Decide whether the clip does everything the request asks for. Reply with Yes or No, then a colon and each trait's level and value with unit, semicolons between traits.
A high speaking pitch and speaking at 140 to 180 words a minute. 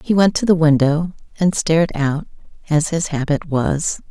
No: medium, 160 Hz; average, 175 wpm